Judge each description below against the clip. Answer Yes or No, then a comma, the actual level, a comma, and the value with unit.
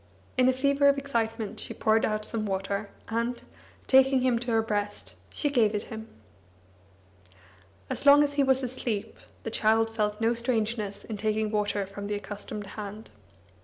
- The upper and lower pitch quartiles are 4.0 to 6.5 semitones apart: No, average, 3.3 semitones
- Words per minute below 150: No, average, 165 wpm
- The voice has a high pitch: Yes, high, 225 Hz